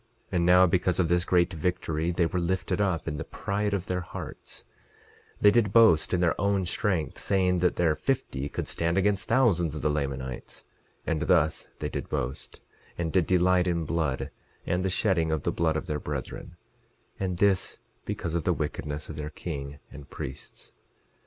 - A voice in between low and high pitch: No, very low, 85 Hz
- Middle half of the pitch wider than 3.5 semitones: No, average, 3.2 semitones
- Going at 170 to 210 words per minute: Yes, average, 185 wpm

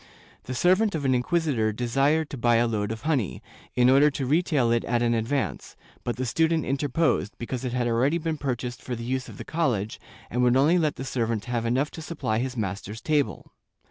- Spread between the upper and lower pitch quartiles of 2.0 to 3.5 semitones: No, average, 4.0 semitones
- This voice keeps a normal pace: No, fast, 210 wpm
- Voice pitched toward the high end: No, low, 125 Hz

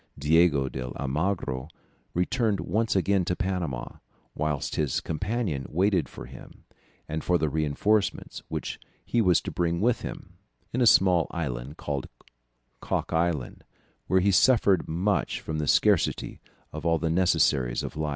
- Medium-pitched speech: No, very low, 85 Hz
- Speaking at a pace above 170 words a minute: No, average, 150 wpm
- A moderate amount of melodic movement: Yes, average, 4.4 semitones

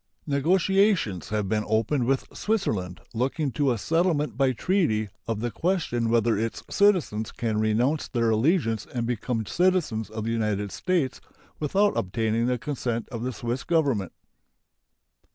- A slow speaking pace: No, average, 145 wpm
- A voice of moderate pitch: No, low, 120 Hz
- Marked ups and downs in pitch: Yes, wide, 6.0 semitones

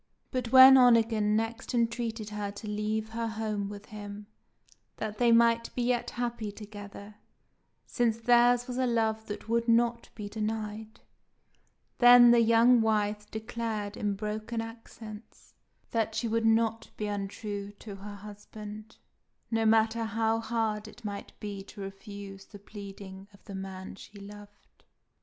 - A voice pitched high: Yes, high, 220 Hz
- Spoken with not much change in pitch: Yes, narrow, 1.9 semitones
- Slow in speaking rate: No, average, 145 wpm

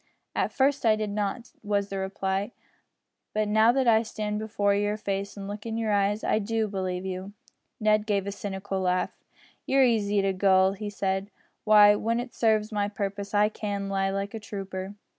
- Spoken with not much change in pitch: Yes, narrow, 1.6 semitones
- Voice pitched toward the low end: No, high, 205 Hz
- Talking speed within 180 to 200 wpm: Yes, average, 190 wpm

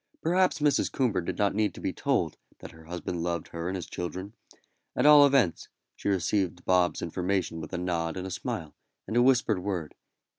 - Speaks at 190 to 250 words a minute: Yes, average, 195 wpm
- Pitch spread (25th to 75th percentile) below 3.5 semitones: No, average, 4.2 semitones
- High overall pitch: No, very low, 95 Hz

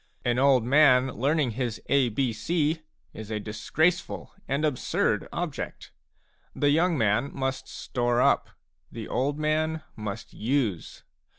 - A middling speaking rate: No, slow, 130 wpm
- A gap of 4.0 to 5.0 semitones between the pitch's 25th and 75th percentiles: Yes, average, 4.7 semitones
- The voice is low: Yes, low, 130 Hz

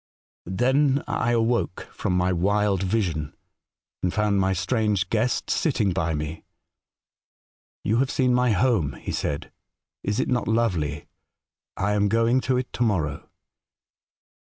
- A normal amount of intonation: Yes, average, 4.9 semitones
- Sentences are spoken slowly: No, average, 150 wpm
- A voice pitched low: Yes, low, 105 Hz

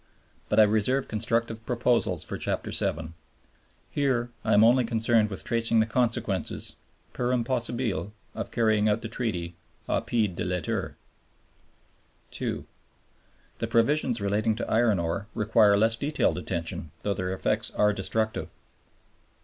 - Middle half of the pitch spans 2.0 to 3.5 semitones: Yes, average, 2.9 semitones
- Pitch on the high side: No, low, 110 Hz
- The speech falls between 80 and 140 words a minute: Yes, slow, 135 wpm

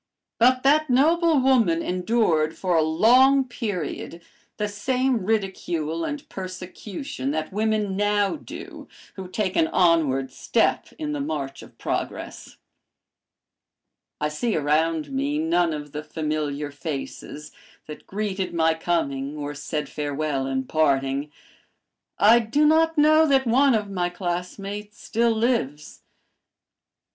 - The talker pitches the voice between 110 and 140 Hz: No, medium, 180 Hz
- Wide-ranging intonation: Yes, wide, 7.2 semitones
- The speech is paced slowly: Yes, slow, 125 wpm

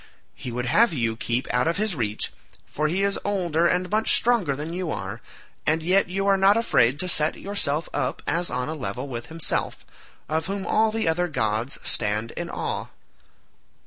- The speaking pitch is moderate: Yes, medium, 160 Hz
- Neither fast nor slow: Yes, average, 190 wpm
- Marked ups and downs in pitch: Yes, wide, 7.5 semitones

